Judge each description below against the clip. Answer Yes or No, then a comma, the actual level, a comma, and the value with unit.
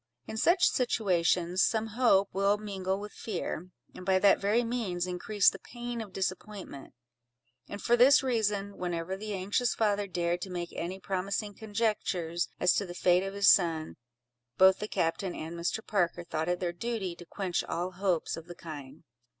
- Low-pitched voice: No, high, 190 Hz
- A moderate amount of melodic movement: Yes, average, 3.1 semitones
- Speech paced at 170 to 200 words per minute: Yes, average, 175 wpm